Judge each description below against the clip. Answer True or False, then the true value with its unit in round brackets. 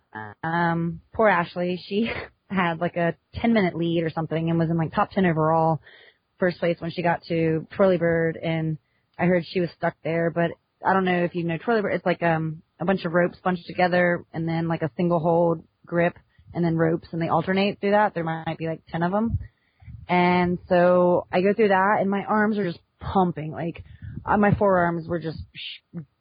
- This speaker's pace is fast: True (210 wpm)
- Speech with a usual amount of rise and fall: False (1.8 semitones)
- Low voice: False (170 Hz)